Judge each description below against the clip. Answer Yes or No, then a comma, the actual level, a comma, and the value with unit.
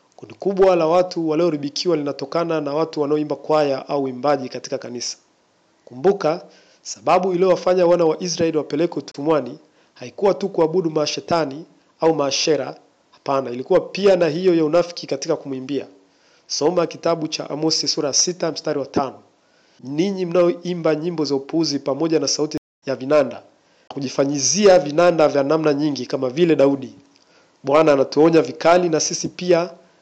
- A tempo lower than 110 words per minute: No, fast, 140 wpm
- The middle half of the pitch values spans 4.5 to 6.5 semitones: No, average, 3.3 semitones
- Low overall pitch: No, medium, 155 Hz